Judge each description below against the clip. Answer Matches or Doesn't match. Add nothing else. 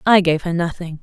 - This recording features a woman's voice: Matches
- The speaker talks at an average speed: Doesn't match